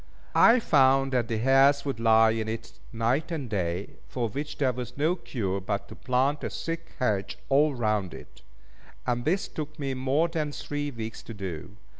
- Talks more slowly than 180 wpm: No, average, 185 wpm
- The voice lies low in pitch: Yes, low, 130 Hz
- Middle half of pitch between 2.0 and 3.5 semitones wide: No, average, 4.6 semitones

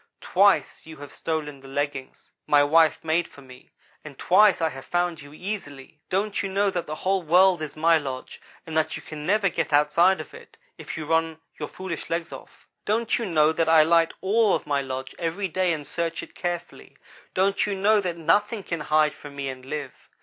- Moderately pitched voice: Yes, medium, 165 Hz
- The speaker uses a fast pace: Yes, fast, 210 wpm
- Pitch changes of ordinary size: Yes, average, 4.1 semitones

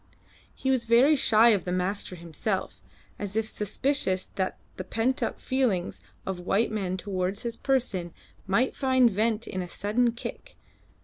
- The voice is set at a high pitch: Yes, high, 210 Hz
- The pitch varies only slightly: No, average, 4.4 semitones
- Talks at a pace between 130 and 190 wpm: Yes, average, 165 wpm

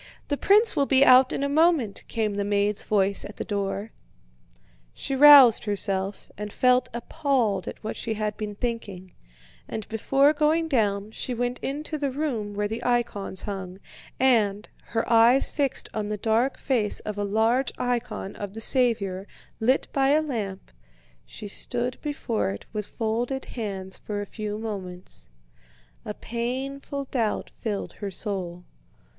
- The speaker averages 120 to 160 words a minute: Yes, average, 155 wpm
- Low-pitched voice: No, high, 225 Hz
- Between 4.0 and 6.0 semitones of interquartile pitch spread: Yes, average, 4.3 semitones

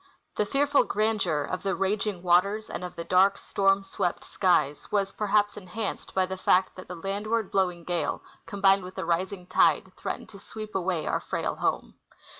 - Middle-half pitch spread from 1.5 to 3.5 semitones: Yes, narrow, 2.4 semitones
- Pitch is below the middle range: No, high, 195 Hz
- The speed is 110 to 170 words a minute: No, average, 180 wpm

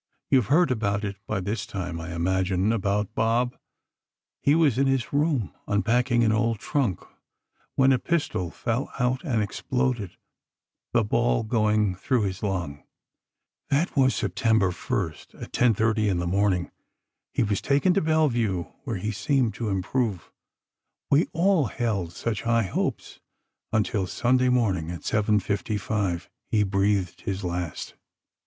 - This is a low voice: Yes, low, 110 Hz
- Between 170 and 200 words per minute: No, slow, 135 wpm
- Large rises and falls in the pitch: No, average, 4.6 semitones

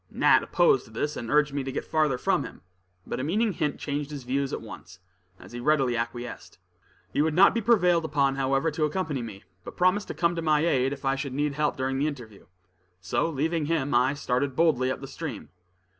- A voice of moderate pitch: Yes, medium, 145 Hz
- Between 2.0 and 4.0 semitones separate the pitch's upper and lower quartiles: Yes, average, 3.5 semitones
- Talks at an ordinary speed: No, fast, 220 wpm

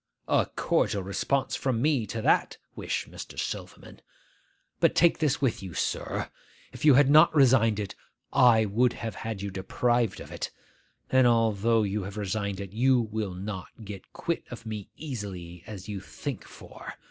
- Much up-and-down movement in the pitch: No, average, 4.1 semitones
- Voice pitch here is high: No, low, 110 Hz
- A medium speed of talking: Yes, average, 170 wpm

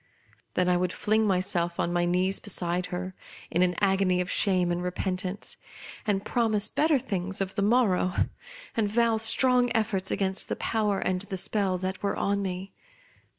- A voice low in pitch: No, high, 190 Hz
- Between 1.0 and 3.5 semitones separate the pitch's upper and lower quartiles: Yes, narrow, 2.5 semitones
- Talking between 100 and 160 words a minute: No, average, 170 wpm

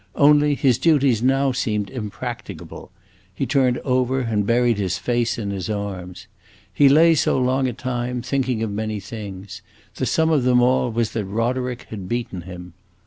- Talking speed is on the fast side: No, average, 170 wpm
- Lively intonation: No, average, 4.0 semitones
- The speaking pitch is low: Yes, low, 120 Hz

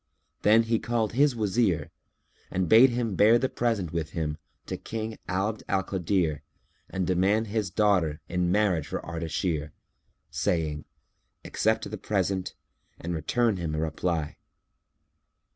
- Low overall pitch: Yes, very low, 95 Hz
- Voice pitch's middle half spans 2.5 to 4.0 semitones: No, average, 5.1 semitones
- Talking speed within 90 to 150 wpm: Yes, slow, 135 wpm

